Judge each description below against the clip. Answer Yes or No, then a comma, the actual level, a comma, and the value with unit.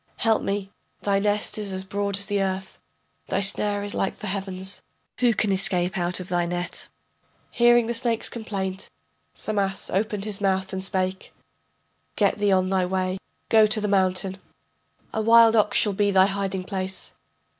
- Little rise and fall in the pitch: Yes, narrow, 1.8 semitones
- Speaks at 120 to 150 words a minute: No, average, 170 wpm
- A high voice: Yes, high, 195 Hz